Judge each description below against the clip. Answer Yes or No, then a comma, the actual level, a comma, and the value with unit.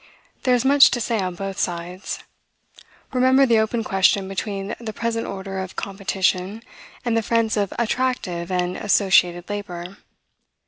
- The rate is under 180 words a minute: Yes, average, 145 wpm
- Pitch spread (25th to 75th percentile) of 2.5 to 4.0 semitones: Yes, average, 3.6 semitones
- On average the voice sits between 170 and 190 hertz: No, high, 200 Hz